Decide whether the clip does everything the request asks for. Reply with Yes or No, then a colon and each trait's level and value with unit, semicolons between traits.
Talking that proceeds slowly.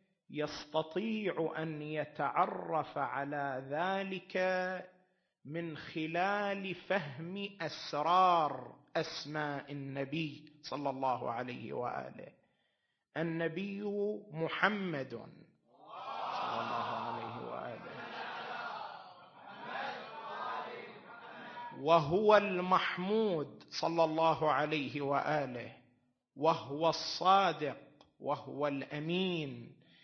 Yes: slow, 60 wpm